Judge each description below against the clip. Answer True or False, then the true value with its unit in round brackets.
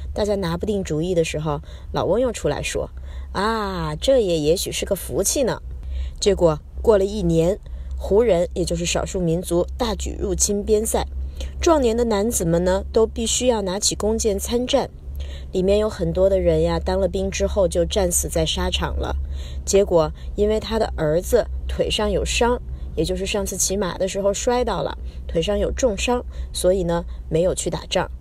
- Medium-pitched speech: True (175 Hz)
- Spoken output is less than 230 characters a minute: False (260 characters per minute)